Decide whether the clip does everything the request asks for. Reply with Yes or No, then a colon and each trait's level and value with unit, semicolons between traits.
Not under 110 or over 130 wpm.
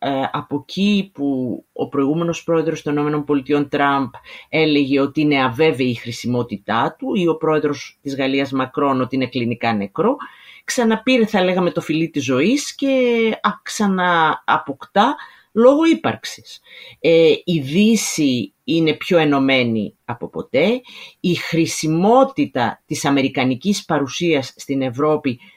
Yes: average, 120 wpm